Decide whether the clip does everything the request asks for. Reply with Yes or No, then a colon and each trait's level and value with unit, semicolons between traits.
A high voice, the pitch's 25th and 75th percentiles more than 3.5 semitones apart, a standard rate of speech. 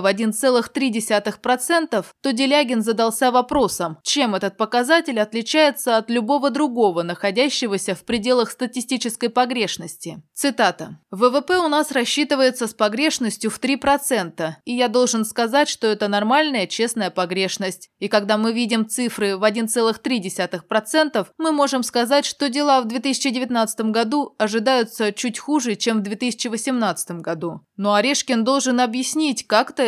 Yes: high, 235 Hz; average, 3.9 semitones; average, 125 wpm